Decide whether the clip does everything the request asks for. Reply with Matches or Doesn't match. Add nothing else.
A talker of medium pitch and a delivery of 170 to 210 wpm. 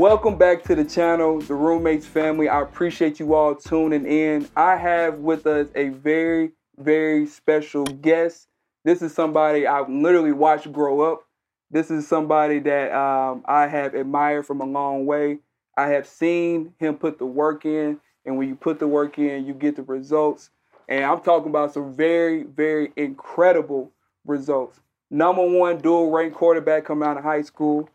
Matches